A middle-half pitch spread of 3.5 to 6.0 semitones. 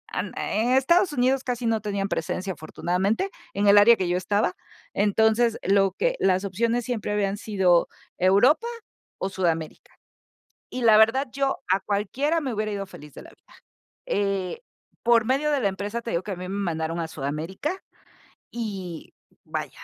Yes: average, 4.2 semitones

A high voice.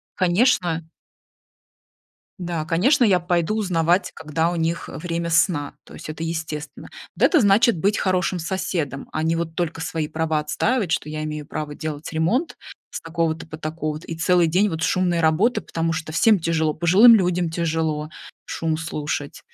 No: medium, 165 Hz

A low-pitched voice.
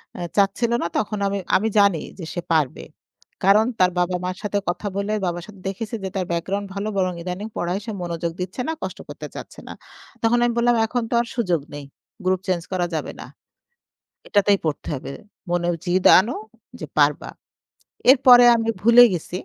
No: high, 190 Hz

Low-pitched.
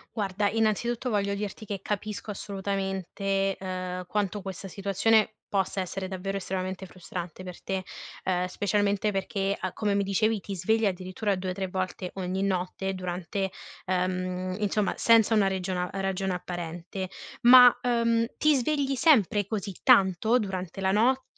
No: high, 195 Hz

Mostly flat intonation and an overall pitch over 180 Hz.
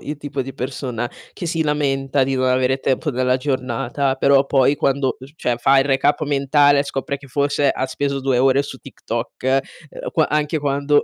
No: narrow, 1.7 semitones; low, 135 Hz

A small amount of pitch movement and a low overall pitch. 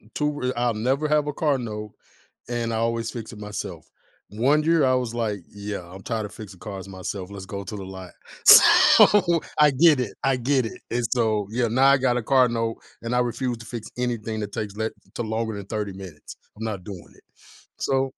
No: average, 3.6 semitones; low, 115 Hz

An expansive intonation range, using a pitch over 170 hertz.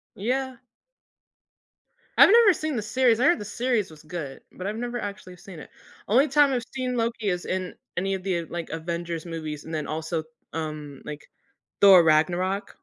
Yes: wide, 6.6 semitones; medium, 185 Hz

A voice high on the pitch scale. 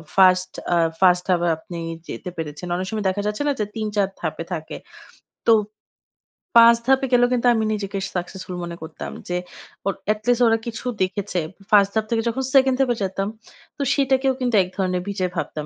Yes: high, 200 Hz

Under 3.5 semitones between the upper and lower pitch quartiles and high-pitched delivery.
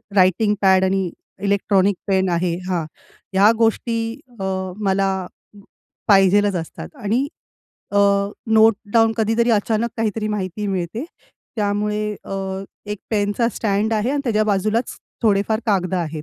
Yes: narrow, 2.5 semitones; high, 205 Hz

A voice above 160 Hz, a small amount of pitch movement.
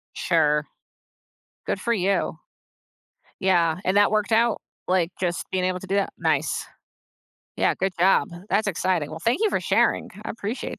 No: medium, 185 Hz; average, 3.2 semitones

